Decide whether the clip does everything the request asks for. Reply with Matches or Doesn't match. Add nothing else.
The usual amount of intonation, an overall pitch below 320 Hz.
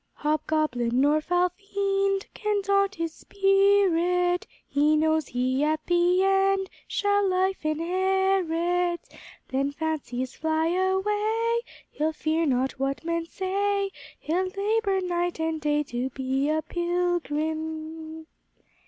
Doesn't match